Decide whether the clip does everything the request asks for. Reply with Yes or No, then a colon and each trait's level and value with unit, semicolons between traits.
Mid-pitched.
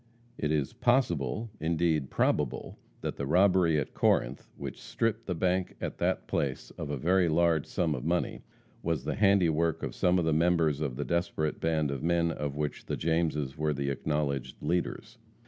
No: very low, 80 Hz